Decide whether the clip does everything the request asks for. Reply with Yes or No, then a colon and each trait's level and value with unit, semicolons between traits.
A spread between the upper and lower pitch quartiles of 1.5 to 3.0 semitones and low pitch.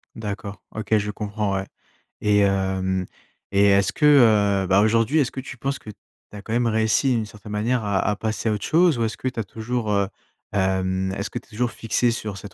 Yes: narrow, 2.5 semitones; low, 105 Hz